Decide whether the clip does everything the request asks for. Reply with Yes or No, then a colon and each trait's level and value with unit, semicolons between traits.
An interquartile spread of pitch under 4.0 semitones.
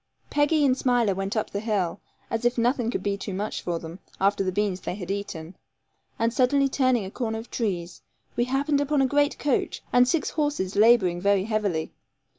No: average, 4.9 semitones